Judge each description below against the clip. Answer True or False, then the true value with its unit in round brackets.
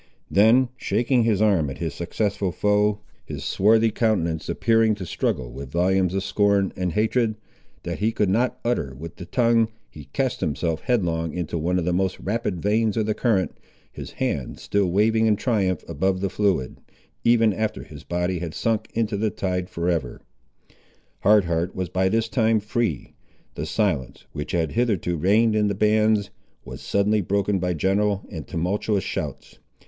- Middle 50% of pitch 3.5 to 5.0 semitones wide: True (4.0 semitones)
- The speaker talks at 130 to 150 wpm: False (175 wpm)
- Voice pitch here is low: True (100 Hz)